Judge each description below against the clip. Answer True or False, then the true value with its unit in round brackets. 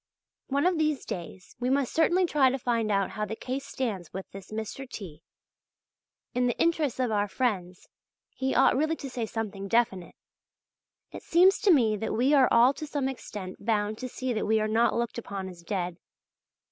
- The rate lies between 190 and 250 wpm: True (195 wpm)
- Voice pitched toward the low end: False (235 Hz)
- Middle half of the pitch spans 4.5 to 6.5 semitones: True (4.8 semitones)